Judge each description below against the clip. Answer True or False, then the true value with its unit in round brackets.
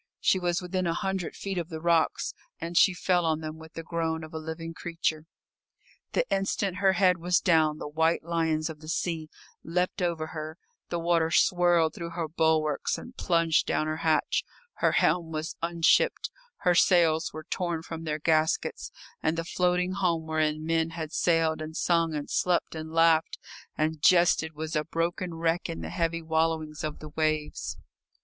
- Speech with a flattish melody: True (1.6 semitones)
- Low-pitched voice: False (165 Hz)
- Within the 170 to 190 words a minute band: True (180 wpm)